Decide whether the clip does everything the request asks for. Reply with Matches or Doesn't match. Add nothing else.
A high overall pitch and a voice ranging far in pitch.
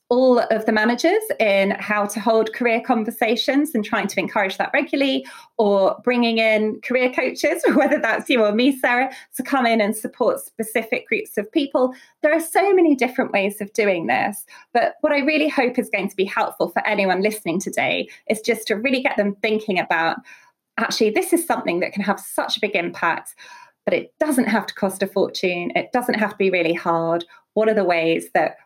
Doesn't match